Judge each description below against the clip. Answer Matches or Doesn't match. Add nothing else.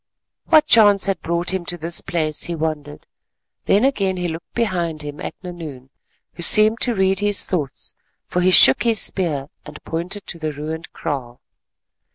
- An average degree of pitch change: Matches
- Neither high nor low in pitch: Matches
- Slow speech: Doesn't match